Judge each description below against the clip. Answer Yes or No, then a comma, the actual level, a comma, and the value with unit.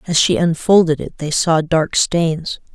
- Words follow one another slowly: No, average, 175 wpm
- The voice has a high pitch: No, medium, 165 Hz